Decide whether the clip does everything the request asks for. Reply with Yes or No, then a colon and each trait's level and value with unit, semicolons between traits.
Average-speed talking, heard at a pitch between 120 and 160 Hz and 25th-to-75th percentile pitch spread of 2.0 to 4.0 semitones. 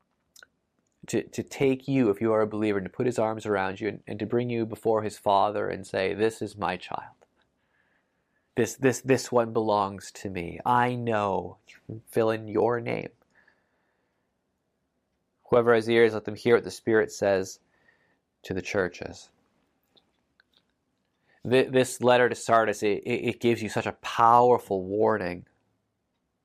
No: average, 155 wpm; low, 110 Hz; narrow, 2.6 semitones